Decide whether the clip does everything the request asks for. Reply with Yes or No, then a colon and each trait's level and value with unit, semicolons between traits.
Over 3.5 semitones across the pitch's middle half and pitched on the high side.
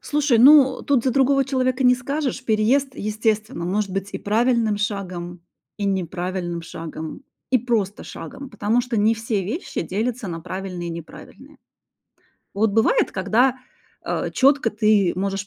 Yes: average, 4.8 semitones; high, 215 Hz